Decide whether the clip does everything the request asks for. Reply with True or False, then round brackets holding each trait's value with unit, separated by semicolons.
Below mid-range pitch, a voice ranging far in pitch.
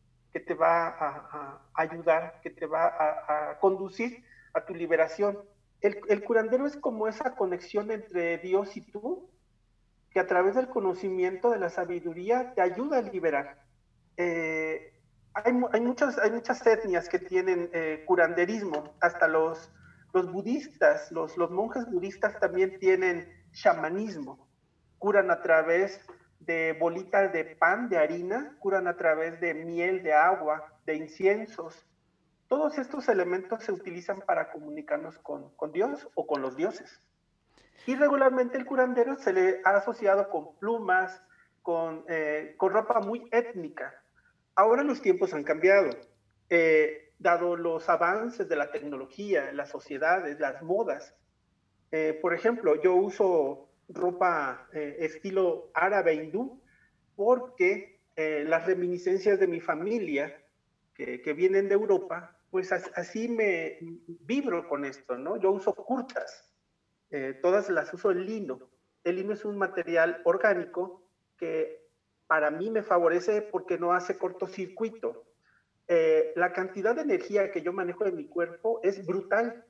False (190 Hz; 5.8 semitones)